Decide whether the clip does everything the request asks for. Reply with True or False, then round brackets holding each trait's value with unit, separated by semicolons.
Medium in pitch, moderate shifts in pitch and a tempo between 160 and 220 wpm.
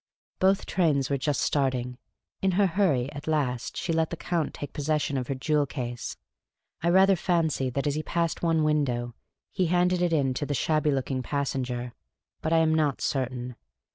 True (150 Hz; 4.1 semitones; 185 wpm)